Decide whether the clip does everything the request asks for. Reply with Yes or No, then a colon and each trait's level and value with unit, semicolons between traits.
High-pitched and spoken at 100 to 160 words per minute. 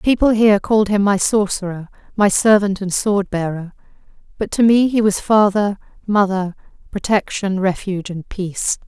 Yes: high, 200 Hz; average, 150 wpm